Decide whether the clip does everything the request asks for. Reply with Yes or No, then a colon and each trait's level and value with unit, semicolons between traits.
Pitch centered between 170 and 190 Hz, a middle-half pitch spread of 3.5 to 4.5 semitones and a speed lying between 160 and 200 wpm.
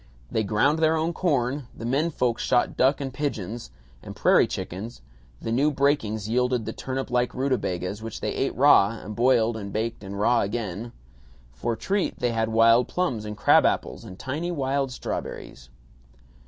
No: low, 120 Hz; average, 3.9 semitones; average, 170 wpm